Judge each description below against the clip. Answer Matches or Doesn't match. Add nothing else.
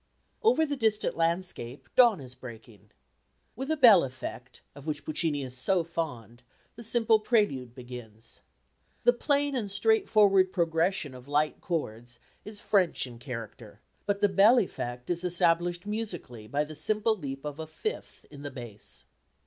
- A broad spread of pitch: Matches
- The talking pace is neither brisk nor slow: Matches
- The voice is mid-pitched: Matches